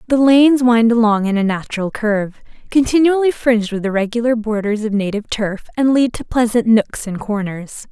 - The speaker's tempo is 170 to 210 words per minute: Yes, average, 175 wpm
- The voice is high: Yes, high, 225 Hz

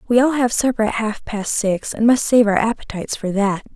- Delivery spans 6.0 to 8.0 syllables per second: No, 5.5 syllables/s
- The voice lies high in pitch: Yes, high, 220 Hz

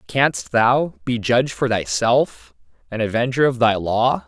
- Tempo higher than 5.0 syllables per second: No, 4.1 syllables/s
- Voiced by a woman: No, male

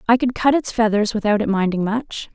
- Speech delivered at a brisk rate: Yes, fast, 230 wpm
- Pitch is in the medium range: No, high, 220 Hz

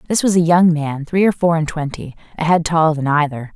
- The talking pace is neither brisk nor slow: No, fast, 255 wpm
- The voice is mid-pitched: Yes, medium, 160 Hz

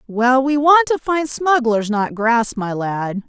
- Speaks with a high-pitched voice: Yes, very high, 250 Hz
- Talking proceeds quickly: No, average, 185 wpm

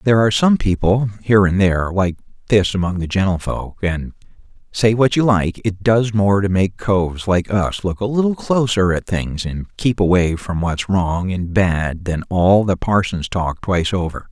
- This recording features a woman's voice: No, male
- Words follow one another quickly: No, average, 195 wpm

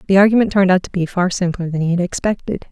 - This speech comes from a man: No, female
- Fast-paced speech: Yes, fast, 265 wpm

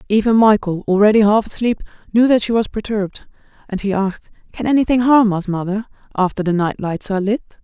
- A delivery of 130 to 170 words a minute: No, average, 190 wpm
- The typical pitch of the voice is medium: No, high, 210 Hz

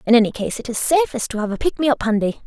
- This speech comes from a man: No, female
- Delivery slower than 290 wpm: No, fast, 315 wpm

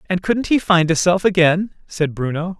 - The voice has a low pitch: No, medium, 175 Hz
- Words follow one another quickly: Yes, fast, 210 wpm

